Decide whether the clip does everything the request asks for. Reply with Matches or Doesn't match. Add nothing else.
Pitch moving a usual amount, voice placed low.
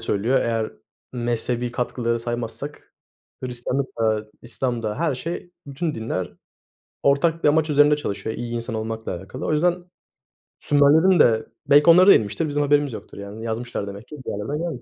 Matches